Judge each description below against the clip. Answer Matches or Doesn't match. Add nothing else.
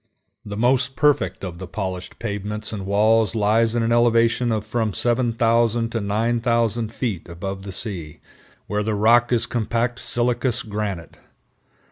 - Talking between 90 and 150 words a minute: Matches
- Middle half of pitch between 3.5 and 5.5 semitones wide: Doesn't match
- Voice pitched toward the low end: Matches